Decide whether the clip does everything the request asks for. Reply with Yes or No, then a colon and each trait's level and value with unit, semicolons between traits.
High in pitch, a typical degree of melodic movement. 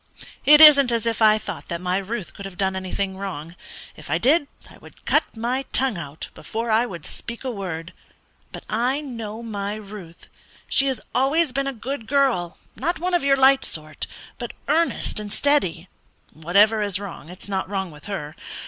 No: high, 215 Hz; wide, 6.1 semitones